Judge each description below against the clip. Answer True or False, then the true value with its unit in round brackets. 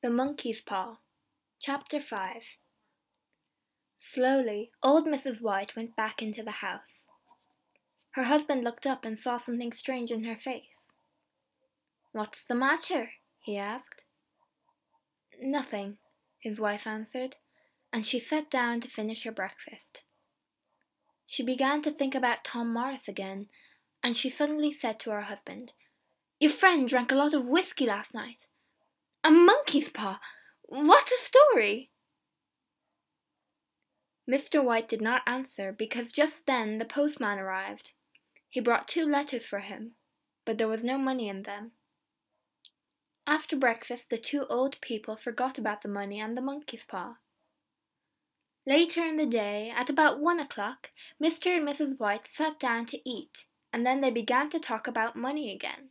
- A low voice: False (250 Hz)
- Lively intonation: False (4.4 semitones)